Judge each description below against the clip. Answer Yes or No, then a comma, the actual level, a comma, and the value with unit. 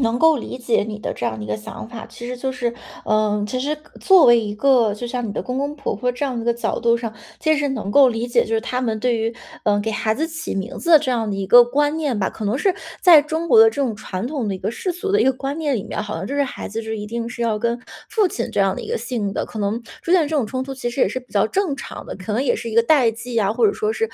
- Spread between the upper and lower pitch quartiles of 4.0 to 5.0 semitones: Yes, average, 4.5 semitones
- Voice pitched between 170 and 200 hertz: No, high, 240 Hz